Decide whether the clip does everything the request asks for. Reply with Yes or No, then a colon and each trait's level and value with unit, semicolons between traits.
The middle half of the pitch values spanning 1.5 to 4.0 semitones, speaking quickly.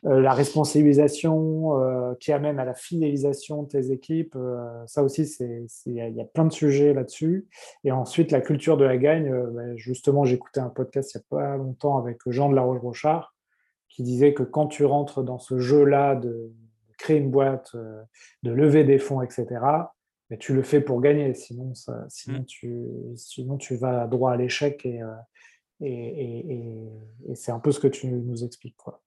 No: average, 2.8 semitones; average, 195 wpm